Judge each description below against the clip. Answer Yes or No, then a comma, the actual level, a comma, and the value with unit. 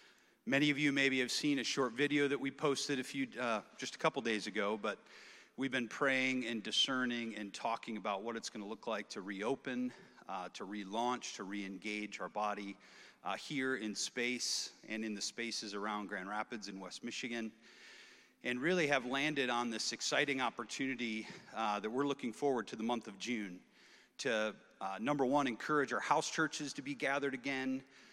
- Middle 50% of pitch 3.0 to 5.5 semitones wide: Yes, average, 4.1 semitones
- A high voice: No, low, 120 Hz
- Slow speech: No, average, 190 wpm